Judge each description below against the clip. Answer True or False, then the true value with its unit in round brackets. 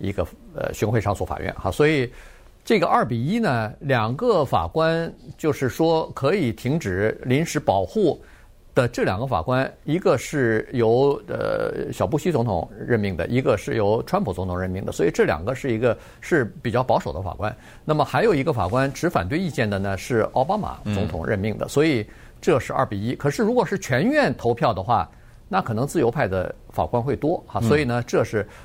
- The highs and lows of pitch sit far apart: True (6.3 semitones)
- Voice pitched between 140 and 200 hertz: False (125 Hz)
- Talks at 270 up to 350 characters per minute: True (290 characters per minute)